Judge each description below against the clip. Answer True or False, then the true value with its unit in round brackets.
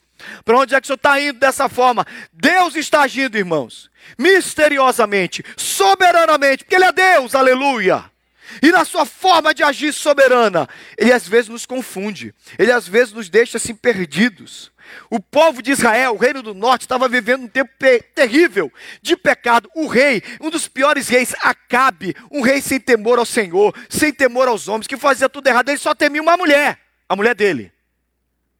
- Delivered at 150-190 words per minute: True (180 wpm)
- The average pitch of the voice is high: True (265 Hz)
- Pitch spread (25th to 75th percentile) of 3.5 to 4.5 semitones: True (4.1 semitones)